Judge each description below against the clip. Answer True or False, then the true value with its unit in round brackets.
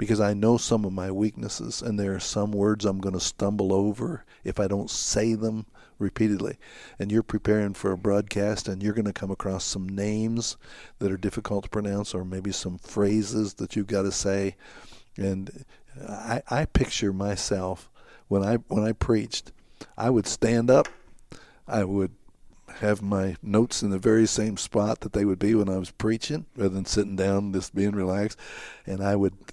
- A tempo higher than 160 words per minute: True (190 wpm)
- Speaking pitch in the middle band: False (100 Hz)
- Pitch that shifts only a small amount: True (1.8 semitones)